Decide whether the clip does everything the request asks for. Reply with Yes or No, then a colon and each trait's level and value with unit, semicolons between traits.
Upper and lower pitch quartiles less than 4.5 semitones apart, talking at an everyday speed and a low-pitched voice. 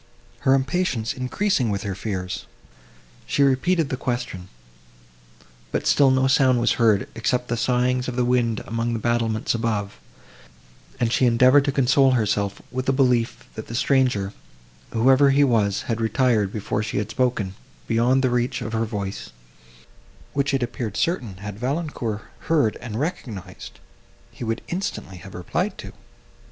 Yes: average, 3.4 semitones; average, 155 wpm; low, 120 Hz